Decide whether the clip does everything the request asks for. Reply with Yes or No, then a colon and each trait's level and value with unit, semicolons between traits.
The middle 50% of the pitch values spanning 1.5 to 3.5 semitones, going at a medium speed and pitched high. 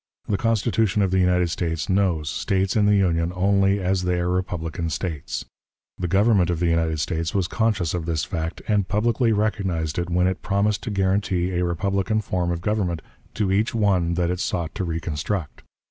No: average, 3.0 semitones; average, 190 wpm; very low, 90 Hz